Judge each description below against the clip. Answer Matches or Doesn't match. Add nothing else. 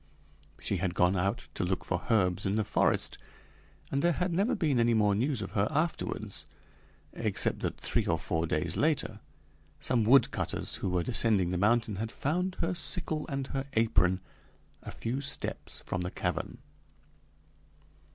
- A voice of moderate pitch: Doesn't match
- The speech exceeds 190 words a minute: Doesn't match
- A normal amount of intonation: Doesn't match